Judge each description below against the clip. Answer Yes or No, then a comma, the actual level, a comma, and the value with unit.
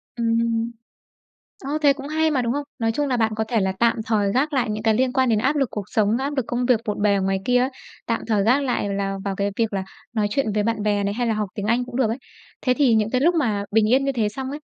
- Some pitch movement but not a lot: Yes, average, 3.7 semitones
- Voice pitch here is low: No, high, 230 Hz